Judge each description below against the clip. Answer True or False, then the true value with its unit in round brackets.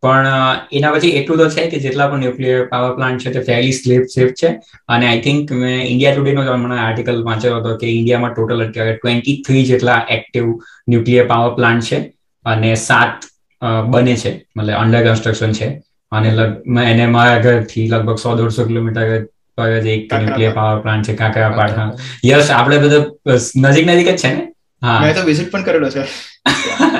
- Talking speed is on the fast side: True (180 wpm)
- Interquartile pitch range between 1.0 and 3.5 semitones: True (2.8 semitones)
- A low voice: True (120 Hz)